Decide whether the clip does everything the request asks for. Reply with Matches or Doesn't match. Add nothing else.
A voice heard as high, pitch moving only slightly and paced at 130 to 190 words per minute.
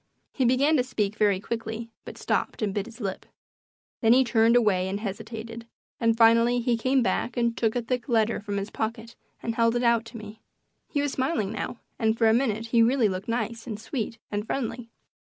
Doesn't match